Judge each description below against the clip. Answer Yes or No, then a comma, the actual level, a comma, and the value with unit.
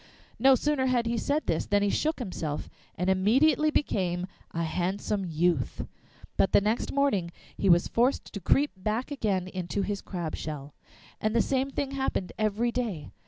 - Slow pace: No, average, 170 wpm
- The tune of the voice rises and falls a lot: Yes, wide, 6.3 semitones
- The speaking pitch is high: Yes, high, 205 Hz